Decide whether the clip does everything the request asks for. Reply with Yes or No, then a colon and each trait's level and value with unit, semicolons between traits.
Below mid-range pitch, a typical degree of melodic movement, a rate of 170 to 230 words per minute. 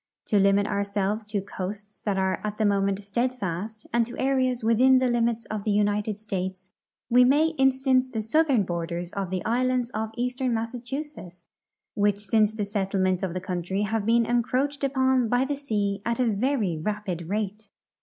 No: high, 215 Hz; average, 3.9 semitones; average, 175 wpm